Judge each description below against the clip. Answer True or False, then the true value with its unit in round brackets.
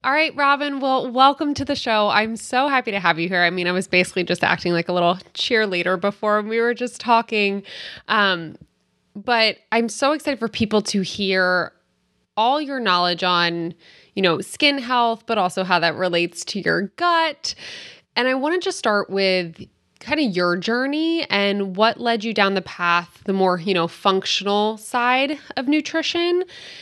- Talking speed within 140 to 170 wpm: False (185 wpm)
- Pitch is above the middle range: True (210 Hz)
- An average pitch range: False (6.2 semitones)